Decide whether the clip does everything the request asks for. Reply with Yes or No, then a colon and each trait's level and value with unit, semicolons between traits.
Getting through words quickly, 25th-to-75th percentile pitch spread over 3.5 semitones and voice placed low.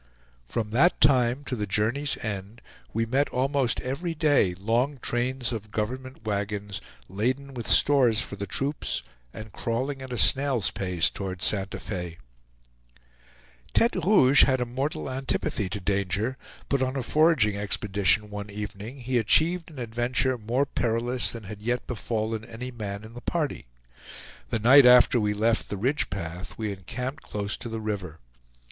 No: average, 160 wpm; average, 4.2 semitones; low, 115 Hz